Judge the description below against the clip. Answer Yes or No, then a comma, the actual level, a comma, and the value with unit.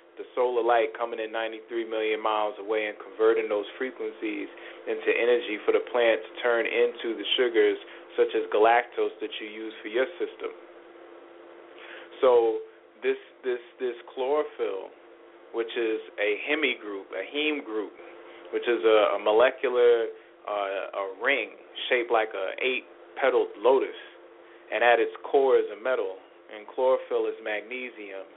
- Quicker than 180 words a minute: No, average, 150 wpm